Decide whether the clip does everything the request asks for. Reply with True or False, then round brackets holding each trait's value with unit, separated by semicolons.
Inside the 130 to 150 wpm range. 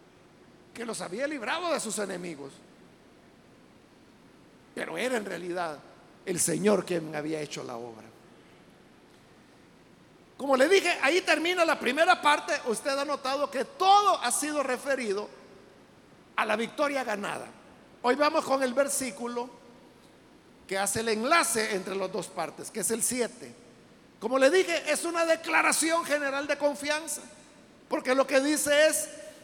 True (140 wpm)